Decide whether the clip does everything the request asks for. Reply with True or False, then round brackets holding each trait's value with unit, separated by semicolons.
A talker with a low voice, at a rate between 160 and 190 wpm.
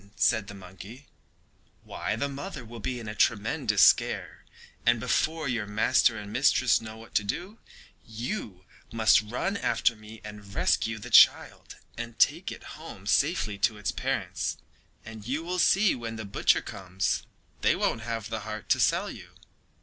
True (110 Hz; 170 wpm)